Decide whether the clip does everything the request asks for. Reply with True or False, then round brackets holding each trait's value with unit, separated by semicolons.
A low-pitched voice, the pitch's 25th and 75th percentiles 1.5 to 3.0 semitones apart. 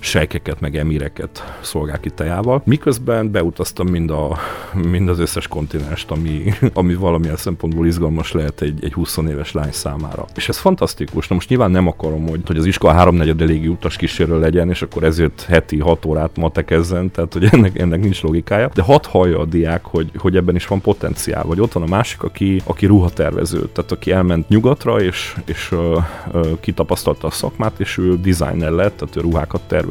True (85 Hz; 2.6 semitones)